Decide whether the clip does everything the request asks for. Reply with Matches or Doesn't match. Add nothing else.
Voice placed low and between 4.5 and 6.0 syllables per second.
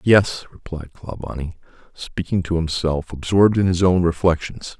Matches